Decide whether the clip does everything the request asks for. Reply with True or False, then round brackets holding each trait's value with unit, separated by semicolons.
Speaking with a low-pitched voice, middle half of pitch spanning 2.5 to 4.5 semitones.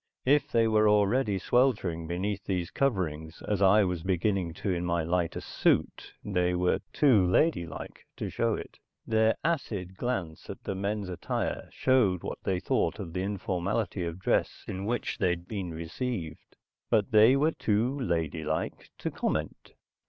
True (95 Hz; 4.0 semitones)